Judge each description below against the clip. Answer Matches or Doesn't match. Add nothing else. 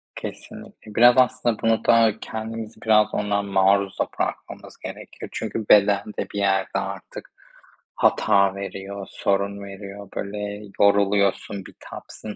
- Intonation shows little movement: Matches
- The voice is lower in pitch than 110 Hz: Matches